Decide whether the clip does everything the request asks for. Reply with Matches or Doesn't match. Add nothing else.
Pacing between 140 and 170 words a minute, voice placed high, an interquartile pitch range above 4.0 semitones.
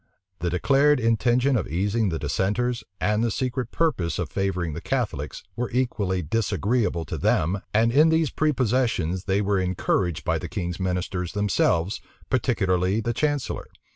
Doesn't match